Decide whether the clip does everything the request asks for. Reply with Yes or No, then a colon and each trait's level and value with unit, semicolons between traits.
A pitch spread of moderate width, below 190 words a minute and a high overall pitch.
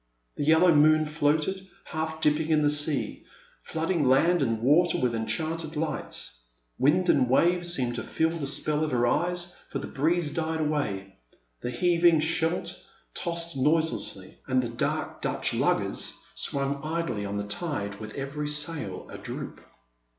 No: average, 3.6 semitones; average, 150 wpm; medium, 150 Hz